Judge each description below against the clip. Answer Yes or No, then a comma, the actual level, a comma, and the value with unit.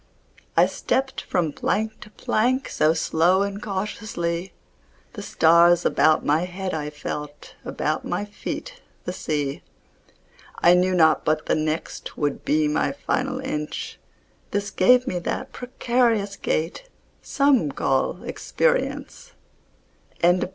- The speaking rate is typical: No, slow, 125 wpm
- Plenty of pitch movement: Yes, wide, 6.3 semitones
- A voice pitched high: No, medium, 180 Hz